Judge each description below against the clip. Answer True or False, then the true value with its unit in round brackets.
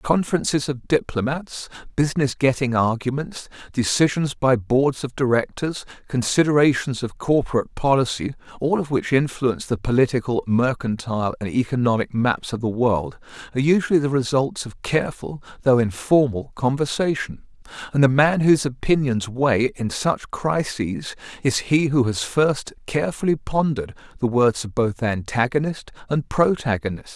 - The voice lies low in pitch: True (130 Hz)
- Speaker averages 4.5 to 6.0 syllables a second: True (5.0 syllables/s)